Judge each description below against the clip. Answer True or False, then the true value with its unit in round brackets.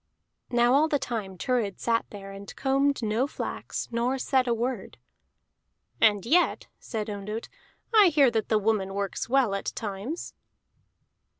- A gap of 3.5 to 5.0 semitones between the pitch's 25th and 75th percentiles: True (4.6 semitones)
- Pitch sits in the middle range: False (230 Hz)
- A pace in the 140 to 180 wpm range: True (145 wpm)